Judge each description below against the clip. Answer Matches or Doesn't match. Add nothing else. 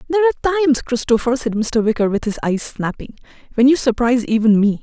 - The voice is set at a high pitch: Matches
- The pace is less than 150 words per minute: Doesn't match